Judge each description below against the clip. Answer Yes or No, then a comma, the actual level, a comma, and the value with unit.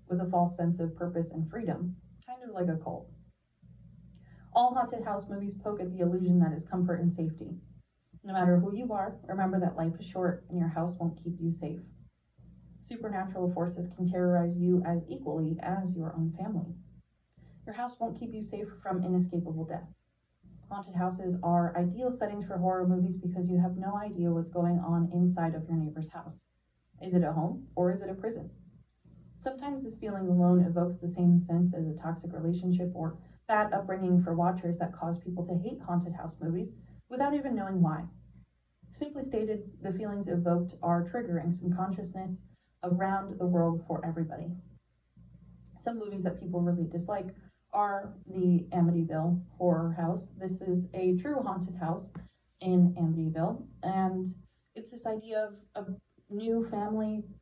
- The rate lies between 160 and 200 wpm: Yes, average, 170 wpm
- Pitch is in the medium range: Yes, medium, 180 Hz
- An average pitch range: No, narrow, 2.3 semitones